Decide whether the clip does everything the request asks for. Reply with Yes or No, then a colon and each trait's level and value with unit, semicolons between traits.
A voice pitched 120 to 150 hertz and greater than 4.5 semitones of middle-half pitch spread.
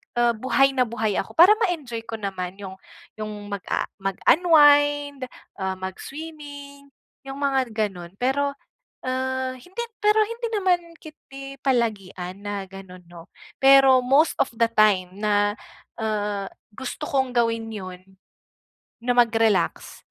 No: high, 245 Hz; wide, 5.6 semitones